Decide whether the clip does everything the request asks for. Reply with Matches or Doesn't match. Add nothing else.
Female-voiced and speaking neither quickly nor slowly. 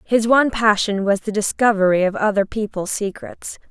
Matches